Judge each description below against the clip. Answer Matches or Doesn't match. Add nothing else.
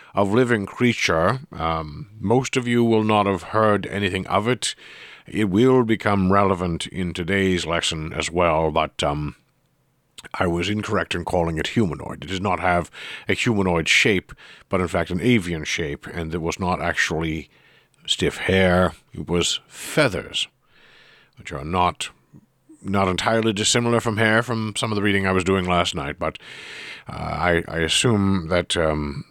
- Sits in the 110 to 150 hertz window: Doesn't match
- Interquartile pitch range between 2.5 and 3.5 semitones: Doesn't match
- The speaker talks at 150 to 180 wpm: Matches